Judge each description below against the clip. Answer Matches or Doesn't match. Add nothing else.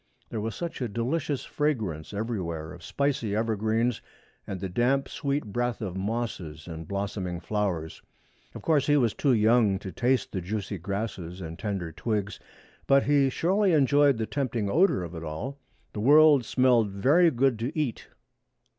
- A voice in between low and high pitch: Doesn't match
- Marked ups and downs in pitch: Matches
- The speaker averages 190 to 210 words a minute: Doesn't match